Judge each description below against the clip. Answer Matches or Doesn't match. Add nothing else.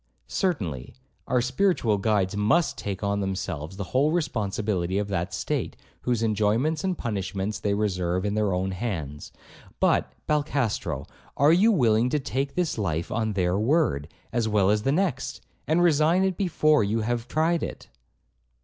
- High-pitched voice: Doesn't match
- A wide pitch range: Matches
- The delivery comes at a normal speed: Matches